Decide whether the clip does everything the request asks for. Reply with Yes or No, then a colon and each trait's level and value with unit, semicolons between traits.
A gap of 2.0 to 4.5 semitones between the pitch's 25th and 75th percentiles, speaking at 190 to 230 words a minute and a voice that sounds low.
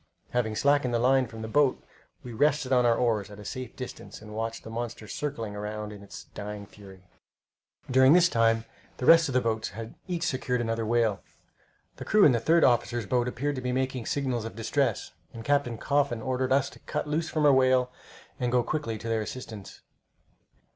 Yes: average, 3.0 semitones; average, 200 wpm; low, 120 Hz